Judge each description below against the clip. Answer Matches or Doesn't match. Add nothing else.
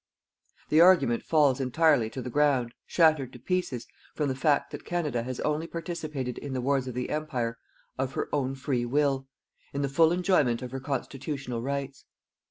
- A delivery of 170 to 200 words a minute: Matches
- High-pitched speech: Doesn't match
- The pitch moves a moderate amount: Matches